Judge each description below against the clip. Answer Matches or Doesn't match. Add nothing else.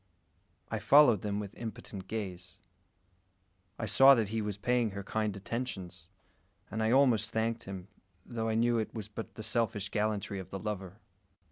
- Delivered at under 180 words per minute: Matches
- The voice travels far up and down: Doesn't match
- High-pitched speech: Doesn't match